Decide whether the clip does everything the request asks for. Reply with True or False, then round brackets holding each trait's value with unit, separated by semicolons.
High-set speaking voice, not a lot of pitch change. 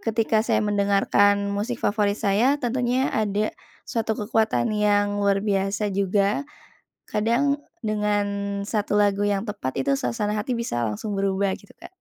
True (205 Hz; 1.7 semitones)